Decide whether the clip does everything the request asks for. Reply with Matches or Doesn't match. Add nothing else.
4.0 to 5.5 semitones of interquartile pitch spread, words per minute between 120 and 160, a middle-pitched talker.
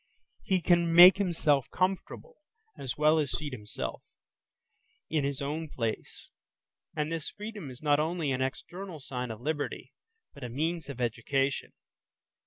Matches